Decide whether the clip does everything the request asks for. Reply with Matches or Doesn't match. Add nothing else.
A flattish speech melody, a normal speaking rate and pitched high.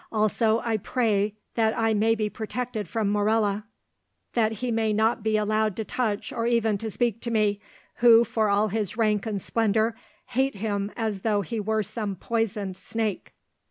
Matches